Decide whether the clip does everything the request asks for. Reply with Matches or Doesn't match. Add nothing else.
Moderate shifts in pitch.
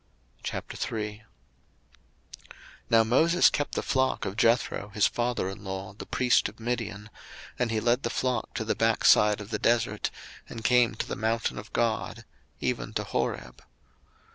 Doesn't match